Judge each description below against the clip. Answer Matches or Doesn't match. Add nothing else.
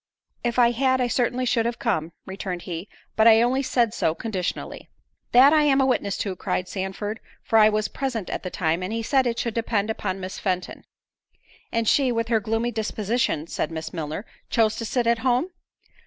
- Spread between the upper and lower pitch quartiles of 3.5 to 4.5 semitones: Matches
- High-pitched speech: Matches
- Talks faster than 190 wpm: Matches